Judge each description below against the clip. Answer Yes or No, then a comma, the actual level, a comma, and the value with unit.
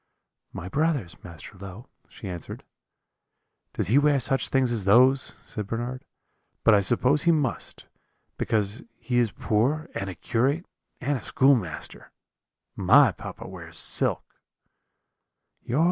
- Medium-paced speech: No, slow, 130 wpm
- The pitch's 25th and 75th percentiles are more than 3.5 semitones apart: Yes, wide, 5.4 semitones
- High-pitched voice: No, low, 120 Hz